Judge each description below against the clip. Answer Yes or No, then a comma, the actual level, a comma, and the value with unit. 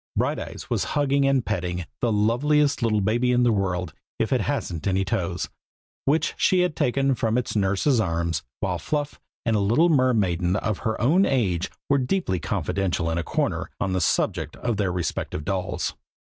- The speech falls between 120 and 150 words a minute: No, average, 175 wpm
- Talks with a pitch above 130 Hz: No, low, 110 Hz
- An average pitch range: No, wide, 6.8 semitones